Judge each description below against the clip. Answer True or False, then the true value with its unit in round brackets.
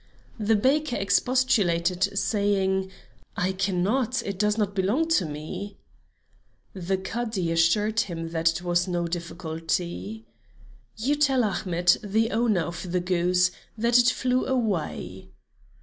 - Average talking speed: False (120 wpm)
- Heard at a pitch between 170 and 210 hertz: True (190 Hz)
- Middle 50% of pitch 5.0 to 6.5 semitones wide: False (4.3 semitones)